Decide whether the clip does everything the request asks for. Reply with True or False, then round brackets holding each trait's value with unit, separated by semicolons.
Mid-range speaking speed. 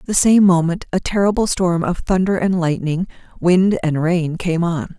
True (180 wpm)